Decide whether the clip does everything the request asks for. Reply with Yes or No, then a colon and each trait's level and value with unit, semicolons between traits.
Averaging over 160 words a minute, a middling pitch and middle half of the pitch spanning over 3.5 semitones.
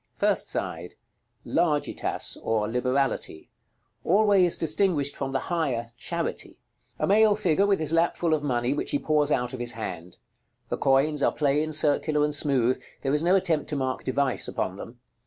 Yes: average, 170 wpm; medium, 145 Hz; average, 4.2 semitones